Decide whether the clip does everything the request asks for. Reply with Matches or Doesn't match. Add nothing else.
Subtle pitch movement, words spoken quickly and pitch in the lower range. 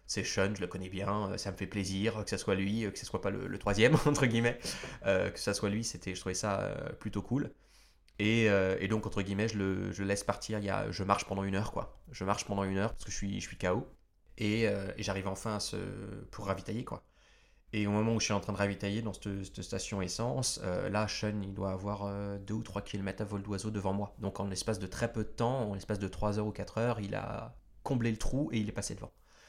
Matches